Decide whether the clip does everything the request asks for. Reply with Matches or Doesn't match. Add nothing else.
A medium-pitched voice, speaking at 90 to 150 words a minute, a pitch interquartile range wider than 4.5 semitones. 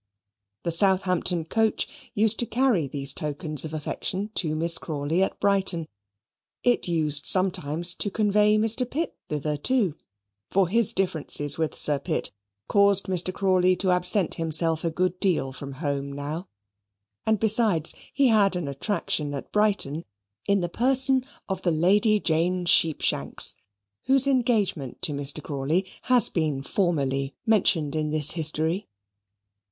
Matches